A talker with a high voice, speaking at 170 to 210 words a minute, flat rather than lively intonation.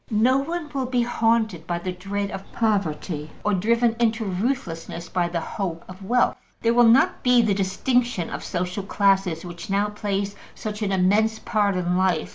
No: high, 200 Hz; average, 180 wpm; average, 4.1 semitones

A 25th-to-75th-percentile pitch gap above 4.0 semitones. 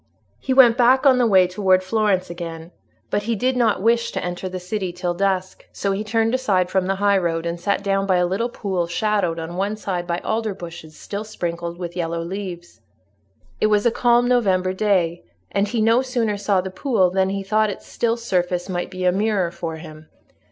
No: average, 3.5 semitones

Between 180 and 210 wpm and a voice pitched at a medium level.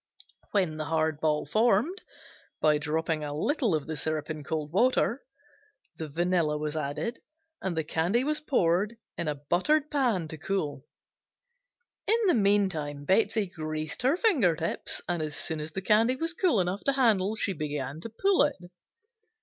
No: average, 165 wpm; medium, 175 Hz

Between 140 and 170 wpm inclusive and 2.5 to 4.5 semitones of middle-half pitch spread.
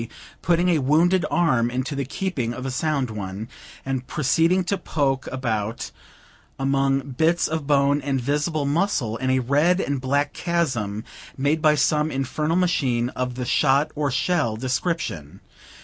Yes: average, 150 wpm; average, 3.8 semitones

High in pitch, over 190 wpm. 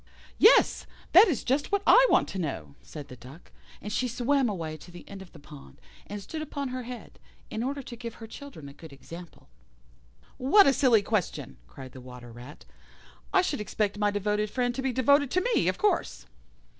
Yes: high, 215 Hz; fast, 205 wpm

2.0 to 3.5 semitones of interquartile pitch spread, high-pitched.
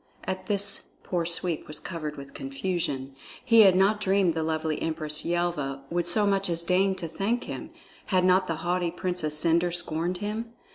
No: average, 3.1 semitones; medium, 175 Hz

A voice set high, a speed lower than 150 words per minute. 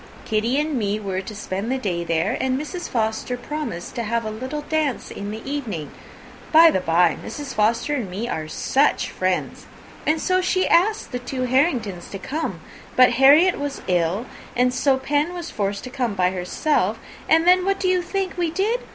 No: very high, 255 Hz; average, 195 wpm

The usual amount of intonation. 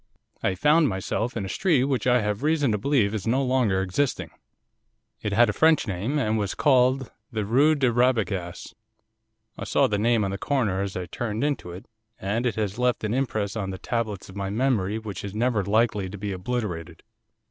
Yes: average, 4.4 semitones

